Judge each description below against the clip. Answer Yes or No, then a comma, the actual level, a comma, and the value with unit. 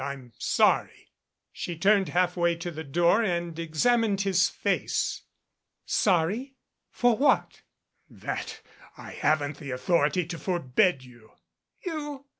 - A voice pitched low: No, medium, 175 Hz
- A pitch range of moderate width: Yes, average, 4.7 semitones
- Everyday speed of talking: No, slow, 120 wpm